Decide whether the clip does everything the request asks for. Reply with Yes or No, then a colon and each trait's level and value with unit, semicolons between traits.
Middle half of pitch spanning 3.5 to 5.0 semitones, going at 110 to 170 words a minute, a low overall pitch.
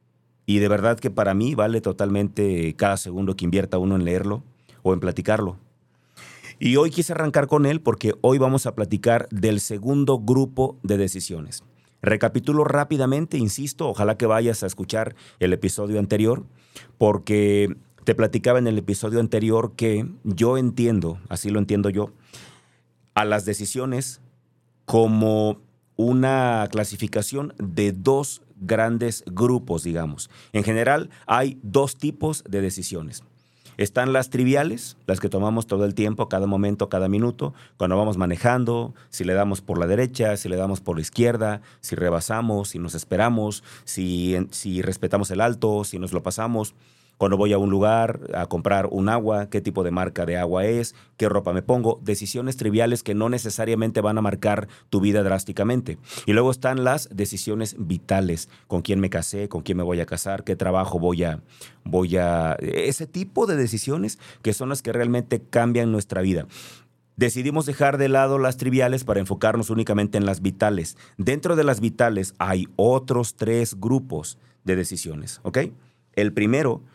Yes: average, 4.0 semitones; average, 165 wpm; low, 105 Hz